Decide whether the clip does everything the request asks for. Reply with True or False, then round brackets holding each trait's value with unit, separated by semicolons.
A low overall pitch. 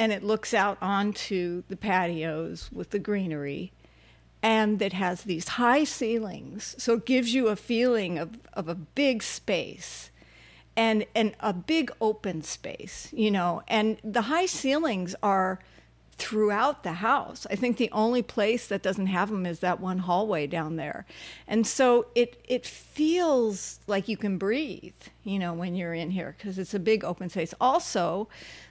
False (210 Hz)